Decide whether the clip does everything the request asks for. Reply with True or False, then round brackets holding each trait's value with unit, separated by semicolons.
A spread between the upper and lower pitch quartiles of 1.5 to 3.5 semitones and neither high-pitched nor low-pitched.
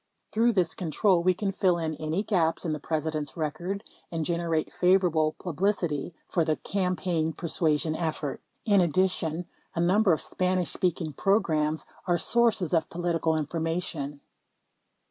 True (2.7 semitones; 170 Hz)